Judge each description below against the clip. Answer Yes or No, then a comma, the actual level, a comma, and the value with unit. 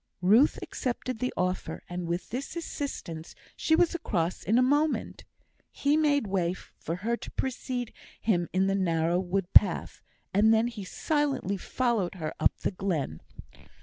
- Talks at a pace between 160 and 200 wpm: No, average, 150 wpm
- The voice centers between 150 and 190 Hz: No, high, 205 Hz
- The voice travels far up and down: Yes, wide, 6.2 semitones